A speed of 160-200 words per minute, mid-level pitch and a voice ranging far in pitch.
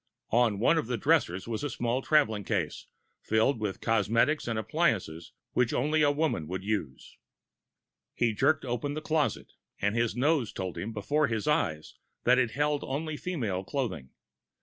No: average, 170 wpm; low, 115 Hz; wide, 5.9 semitones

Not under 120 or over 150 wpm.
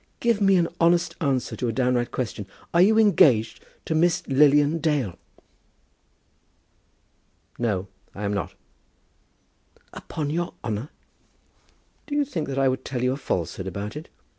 Yes: average, 145 wpm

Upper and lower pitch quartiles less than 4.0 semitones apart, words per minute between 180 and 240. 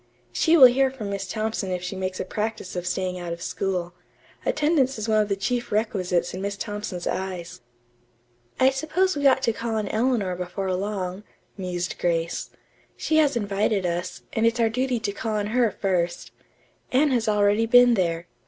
No: average, 4.5 semitones; average, 185 wpm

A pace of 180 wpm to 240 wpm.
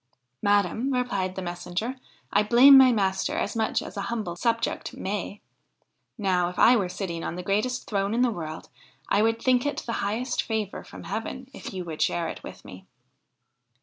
Yes: average, 195 wpm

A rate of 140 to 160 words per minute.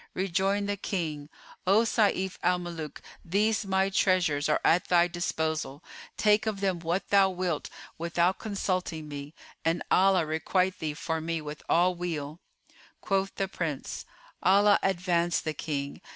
Yes: average, 145 wpm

